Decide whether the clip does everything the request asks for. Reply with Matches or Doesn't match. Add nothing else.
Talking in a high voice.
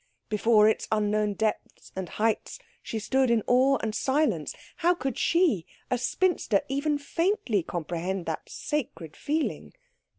Matches